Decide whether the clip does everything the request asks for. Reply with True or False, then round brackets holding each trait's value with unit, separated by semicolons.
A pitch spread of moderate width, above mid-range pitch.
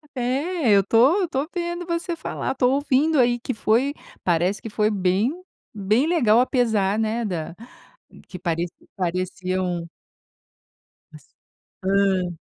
False (6.2 semitones; 215 Hz)